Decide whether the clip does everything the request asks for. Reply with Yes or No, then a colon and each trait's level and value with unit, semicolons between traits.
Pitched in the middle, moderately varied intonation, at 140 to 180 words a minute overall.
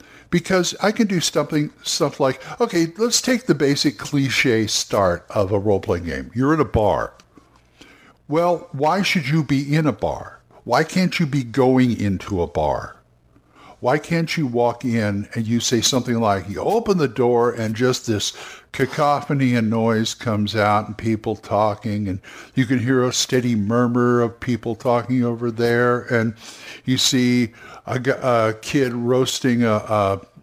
No: low, 125 Hz; average, 4.6 semitones; average, 170 wpm